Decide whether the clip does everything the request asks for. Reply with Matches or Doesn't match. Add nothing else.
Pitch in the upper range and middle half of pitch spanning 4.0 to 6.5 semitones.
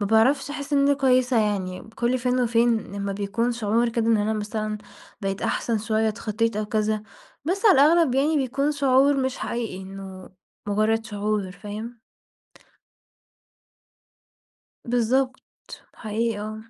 Doesn't match